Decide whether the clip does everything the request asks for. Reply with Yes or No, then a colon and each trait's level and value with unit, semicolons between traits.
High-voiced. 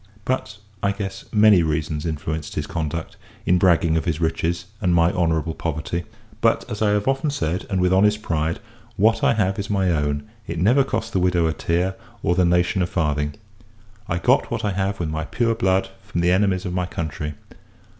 No: very low, 90 Hz